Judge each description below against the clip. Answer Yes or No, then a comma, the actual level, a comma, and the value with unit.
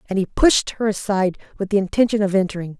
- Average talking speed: No, fast, 215 wpm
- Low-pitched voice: No, high, 200 Hz